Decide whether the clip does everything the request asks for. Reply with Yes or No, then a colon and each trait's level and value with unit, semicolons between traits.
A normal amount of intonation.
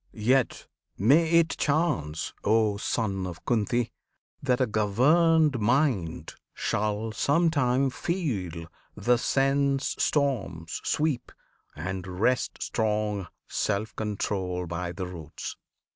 No: wide, 6.4 semitones